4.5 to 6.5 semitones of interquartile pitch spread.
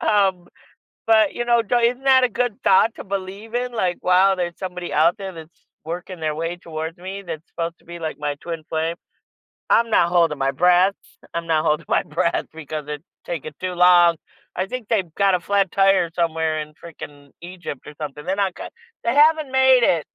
No: average, 3.5 semitones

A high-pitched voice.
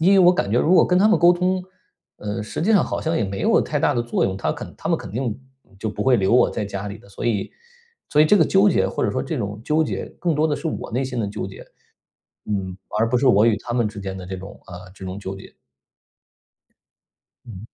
No: low, 115 Hz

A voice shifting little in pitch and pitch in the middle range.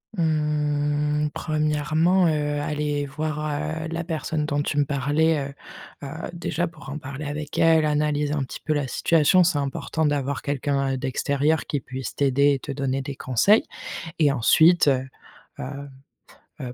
Yes: narrow, 1.9 semitones; medium, 145 Hz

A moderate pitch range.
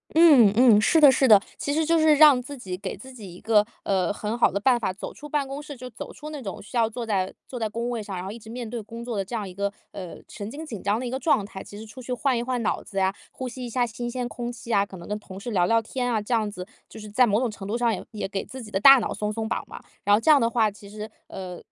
Yes: average, 3.7 semitones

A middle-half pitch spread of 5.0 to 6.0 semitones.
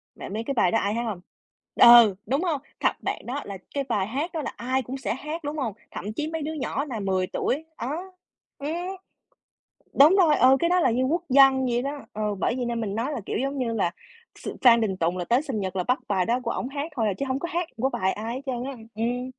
No: average, 4.4 semitones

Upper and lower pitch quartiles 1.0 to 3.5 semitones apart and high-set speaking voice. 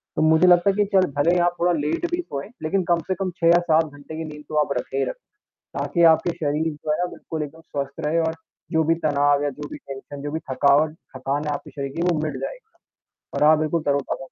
No: average, 2.9 semitones; medium, 155 Hz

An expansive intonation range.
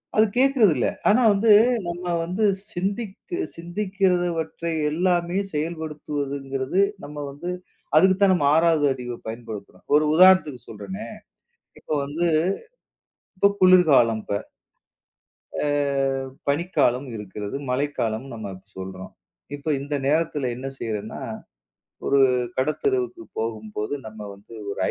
Yes: wide, 7.2 semitones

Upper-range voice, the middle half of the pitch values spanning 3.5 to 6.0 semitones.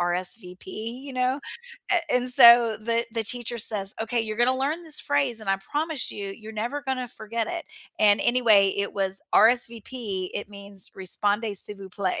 Yes: high, 225 Hz; average, 3.9 semitones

